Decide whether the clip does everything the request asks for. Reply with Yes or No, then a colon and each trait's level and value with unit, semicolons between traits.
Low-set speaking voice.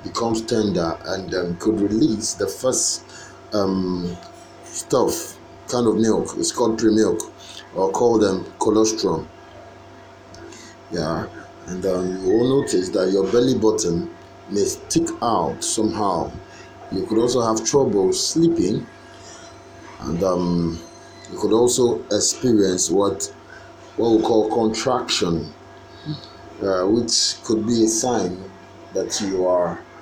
Yes: low, 110 Hz